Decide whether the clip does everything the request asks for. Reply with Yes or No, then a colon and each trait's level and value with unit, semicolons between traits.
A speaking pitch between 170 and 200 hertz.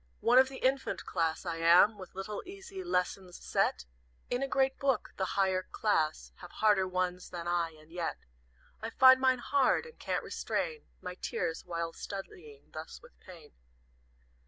Yes: high, 190 Hz